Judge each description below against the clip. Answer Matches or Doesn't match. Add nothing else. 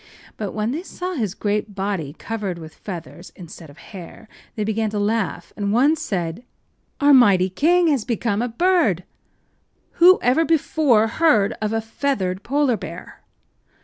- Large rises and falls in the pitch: Matches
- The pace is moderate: Matches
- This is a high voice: Matches